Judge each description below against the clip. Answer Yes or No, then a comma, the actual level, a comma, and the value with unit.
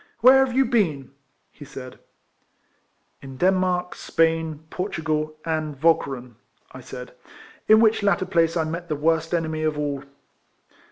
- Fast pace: No, average, 155 wpm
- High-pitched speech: No, medium, 160 Hz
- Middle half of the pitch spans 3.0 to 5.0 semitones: Yes, average, 3.4 semitones